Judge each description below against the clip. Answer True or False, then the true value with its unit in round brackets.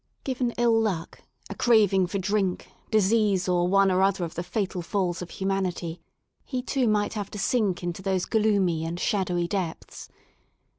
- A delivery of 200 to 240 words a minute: False (165 wpm)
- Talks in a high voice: True (195 Hz)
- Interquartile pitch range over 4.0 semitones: False (3.1 semitones)